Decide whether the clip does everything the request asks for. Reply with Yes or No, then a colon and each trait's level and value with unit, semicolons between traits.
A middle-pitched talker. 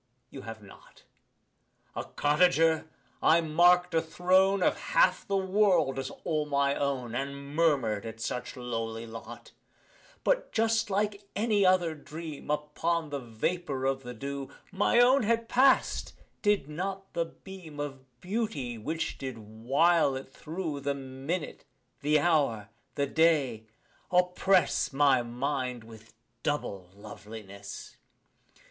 Yes: medium, 150 Hz